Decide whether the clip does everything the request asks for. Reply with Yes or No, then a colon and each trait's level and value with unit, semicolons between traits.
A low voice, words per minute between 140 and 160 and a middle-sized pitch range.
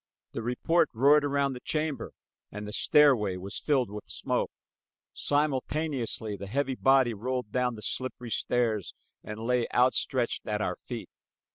Yes: low, 125 Hz; average, 145 wpm; average, 4.2 semitones